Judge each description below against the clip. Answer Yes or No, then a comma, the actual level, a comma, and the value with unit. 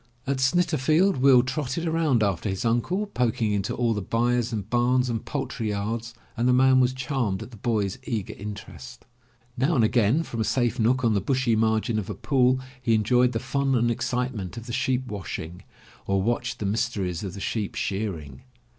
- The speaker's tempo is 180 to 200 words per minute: Yes, average, 195 wpm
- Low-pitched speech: Yes, low, 120 Hz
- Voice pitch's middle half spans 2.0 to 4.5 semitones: Yes, average, 3.6 semitones